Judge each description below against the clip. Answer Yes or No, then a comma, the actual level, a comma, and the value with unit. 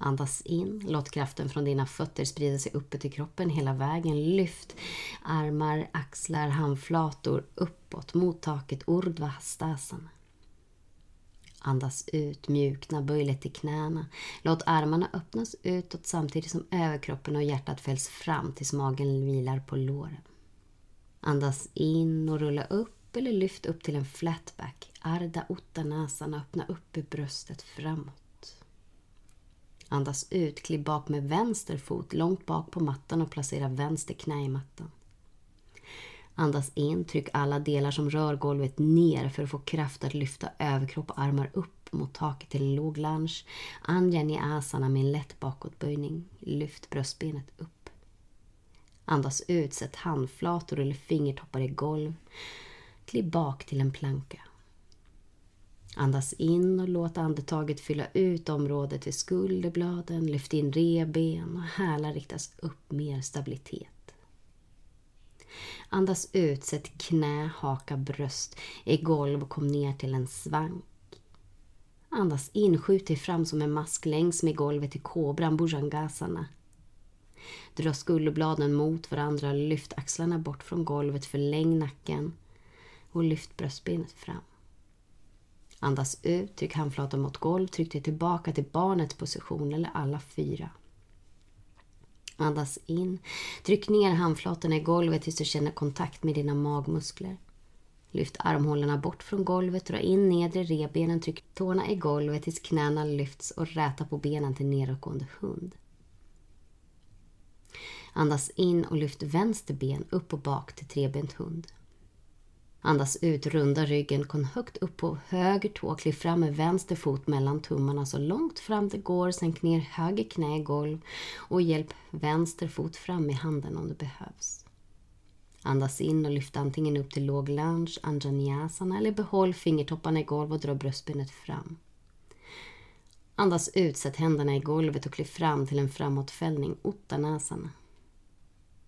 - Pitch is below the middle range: No, medium, 150 Hz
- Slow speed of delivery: No, average, 140 wpm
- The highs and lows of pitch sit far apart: No, average, 3.1 semitones